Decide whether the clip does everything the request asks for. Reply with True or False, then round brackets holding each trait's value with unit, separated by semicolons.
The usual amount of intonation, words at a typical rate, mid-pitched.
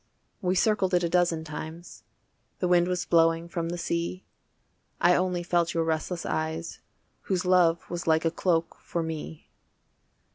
False (1.5 semitones; 155 wpm; 170 Hz)